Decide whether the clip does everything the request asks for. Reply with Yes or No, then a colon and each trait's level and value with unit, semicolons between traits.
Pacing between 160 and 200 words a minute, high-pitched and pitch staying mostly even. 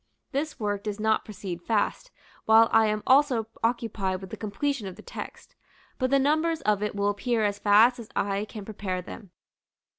No: average, 185 wpm; high, 215 Hz; average, 3.2 semitones